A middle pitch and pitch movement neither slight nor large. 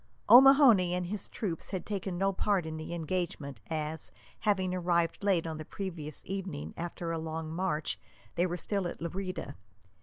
Yes: medium, 175 Hz; average, 3.0 semitones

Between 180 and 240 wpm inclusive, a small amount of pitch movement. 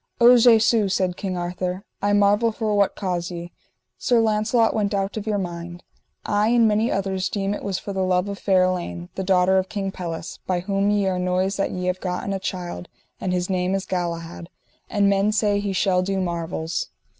Yes: fast, 205 wpm; narrow, 2.2 semitones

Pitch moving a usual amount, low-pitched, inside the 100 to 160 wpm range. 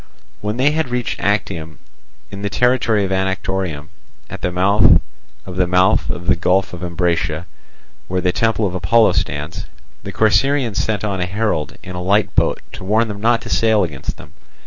No: average, 3.5 semitones; very low, 95 Hz; average, 185 wpm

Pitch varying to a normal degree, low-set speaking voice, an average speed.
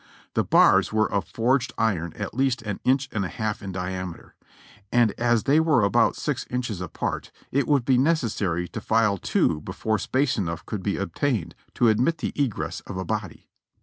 Yes: average, 4.8 semitones; low, 110 Hz; average, 185 wpm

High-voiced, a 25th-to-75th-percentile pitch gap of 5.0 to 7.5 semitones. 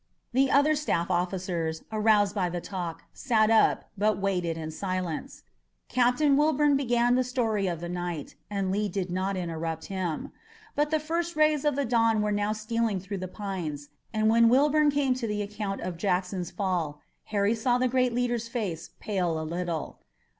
Yes: high, 205 Hz; wide, 5.5 semitones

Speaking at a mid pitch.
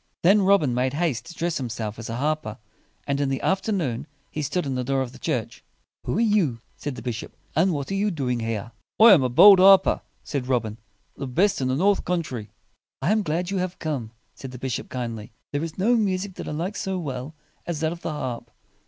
Yes: medium, 150 Hz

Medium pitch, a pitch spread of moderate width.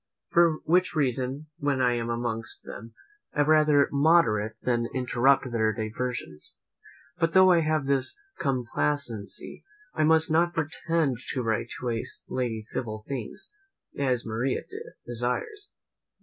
No: low, 130 Hz; average, 4.8 semitones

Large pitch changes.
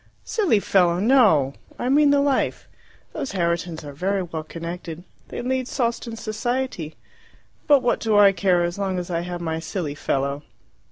Yes: wide, 6.3 semitones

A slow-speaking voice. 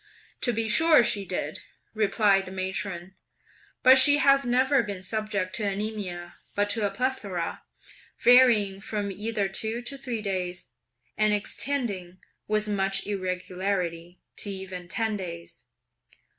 Yes: slow, 130 wpm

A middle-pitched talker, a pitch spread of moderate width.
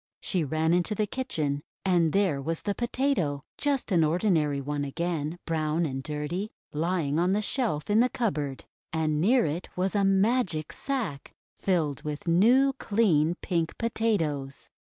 No: medium, 170 Hz; wide, 5.7 semitones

